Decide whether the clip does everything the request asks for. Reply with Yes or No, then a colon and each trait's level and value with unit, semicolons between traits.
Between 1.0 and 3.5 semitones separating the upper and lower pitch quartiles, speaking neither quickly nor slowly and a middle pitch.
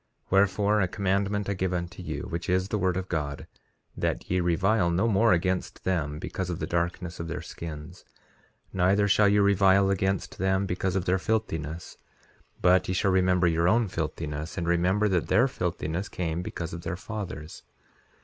No: narrow, 2.4 semitones; average, 180 wpm; very low, 90 Hz